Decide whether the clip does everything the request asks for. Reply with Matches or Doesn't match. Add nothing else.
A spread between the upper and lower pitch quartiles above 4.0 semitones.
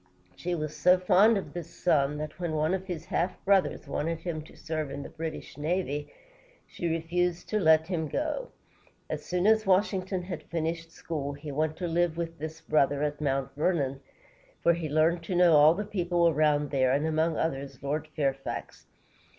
Doesn't match